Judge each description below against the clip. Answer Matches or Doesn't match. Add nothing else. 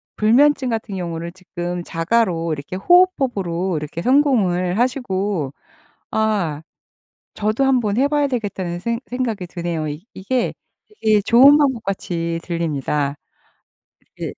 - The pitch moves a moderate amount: Doesn't match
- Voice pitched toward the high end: Matches